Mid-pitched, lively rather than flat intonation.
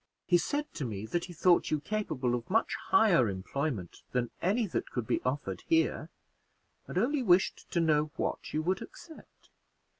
Yes: medium, 165 Hz; wide, 8.1 semitones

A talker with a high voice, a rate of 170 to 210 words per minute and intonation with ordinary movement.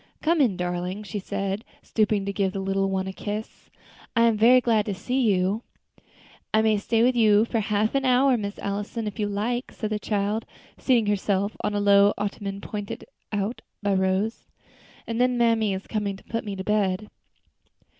No: high, 210 Hz; average, 190 wpm; narrow, 2.3 semitones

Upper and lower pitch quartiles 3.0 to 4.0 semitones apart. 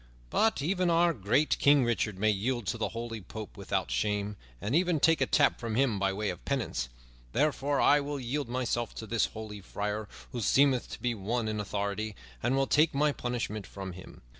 No: average, 5.1 semitones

